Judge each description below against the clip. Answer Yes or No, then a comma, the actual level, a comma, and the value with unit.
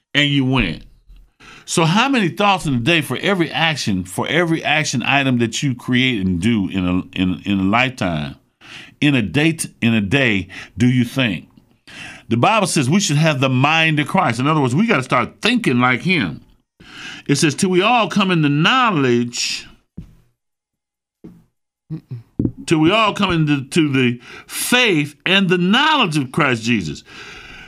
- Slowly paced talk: No, average, 170 wpm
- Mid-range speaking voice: Yes, medium, 145 Hz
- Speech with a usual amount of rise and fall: No, wide, 5.9 semitones